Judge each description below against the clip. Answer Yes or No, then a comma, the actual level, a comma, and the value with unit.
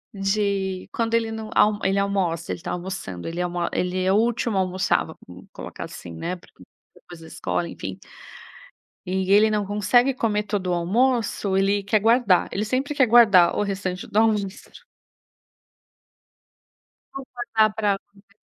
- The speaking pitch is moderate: No, high, 200 Hz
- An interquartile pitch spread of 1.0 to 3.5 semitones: Yes, average, 3.1 semitones